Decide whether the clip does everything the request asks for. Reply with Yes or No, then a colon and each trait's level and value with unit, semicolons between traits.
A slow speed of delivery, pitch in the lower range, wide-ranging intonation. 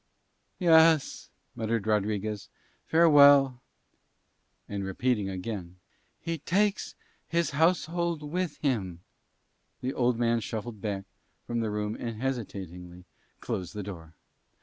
Yes: slow, 105 wpm; low, 115 Hz; wide, 6.7 semitones